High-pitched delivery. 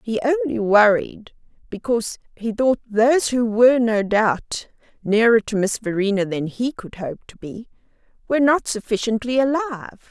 Yes: high, 230 Hz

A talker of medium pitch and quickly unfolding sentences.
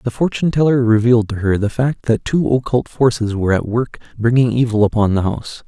No: low, 120 Hz; fast, 210 wpm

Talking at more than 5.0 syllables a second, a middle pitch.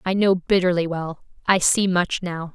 No: 4.5 syllables/s; medium, 180 Hz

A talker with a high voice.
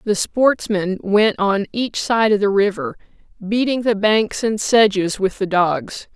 Yes: high, 210 Hz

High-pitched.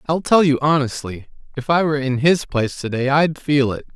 No: medium, 140 Hz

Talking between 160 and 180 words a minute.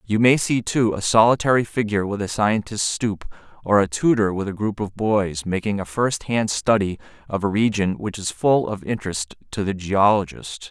No: average, 190 wpm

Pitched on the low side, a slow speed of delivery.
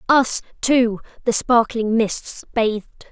No: high, 230 Hz; slow, 115 wpm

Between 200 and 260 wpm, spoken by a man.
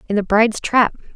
No: fast, 205 wpm; female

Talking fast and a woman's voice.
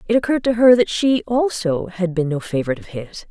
Yes: fast, 235 wpm; female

